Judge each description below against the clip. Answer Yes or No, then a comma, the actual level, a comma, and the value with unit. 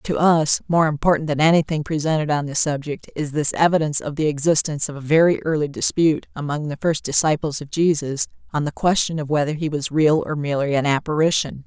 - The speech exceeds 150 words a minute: Yes, average, 200 wpm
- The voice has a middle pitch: Yes, medium, 150 Hz